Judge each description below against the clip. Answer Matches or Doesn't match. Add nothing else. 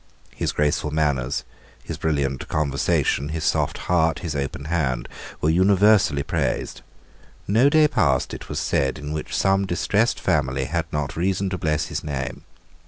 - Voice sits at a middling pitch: Doesn't match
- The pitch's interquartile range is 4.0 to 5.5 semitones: Matches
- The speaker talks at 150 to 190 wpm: Matches